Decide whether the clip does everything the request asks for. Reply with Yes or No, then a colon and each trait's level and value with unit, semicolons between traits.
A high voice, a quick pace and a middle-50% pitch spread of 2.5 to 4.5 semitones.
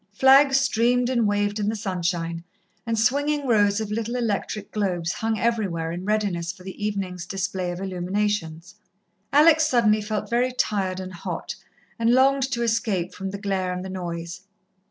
No: high, 205 Hz; average, 165 wpm; average, 4.1 semitones